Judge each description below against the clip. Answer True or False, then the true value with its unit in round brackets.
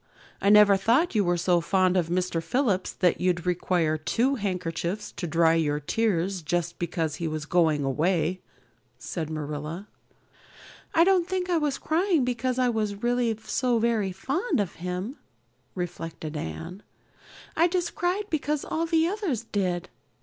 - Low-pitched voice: False (190 Hz)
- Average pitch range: False (7.0 semitones)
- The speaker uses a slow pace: False (155 wpm)